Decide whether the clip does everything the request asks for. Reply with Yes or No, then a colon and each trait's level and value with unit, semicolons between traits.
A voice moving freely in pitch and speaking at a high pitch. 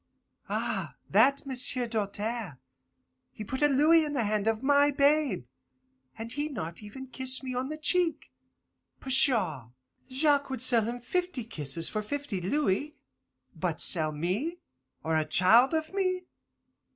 Yes: wide, 5.8 semitones; very high, 255 Hz